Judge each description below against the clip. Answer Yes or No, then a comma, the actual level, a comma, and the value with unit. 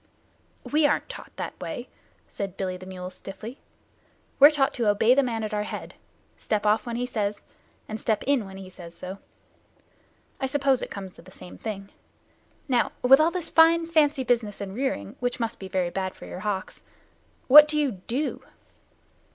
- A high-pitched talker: Yes, high, 220 Hz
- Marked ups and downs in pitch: Yes, wide, 5.8 semitones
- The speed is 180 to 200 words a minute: Yes, average, 190 wpm